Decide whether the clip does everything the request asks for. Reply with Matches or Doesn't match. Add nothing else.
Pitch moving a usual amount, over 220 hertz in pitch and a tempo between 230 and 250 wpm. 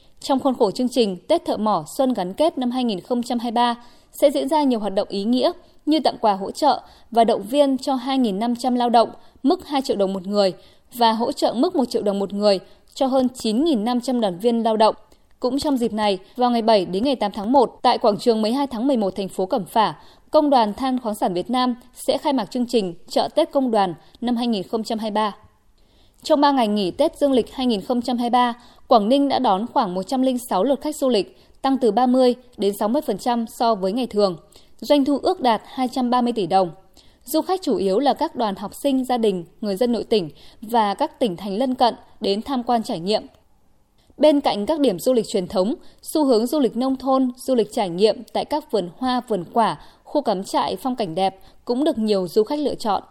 Doesn't match